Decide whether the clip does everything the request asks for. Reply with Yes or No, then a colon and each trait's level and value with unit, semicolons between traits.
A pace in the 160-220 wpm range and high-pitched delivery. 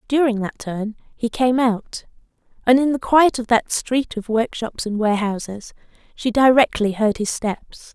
Yes: average, 165 wpm; high, 230 Hz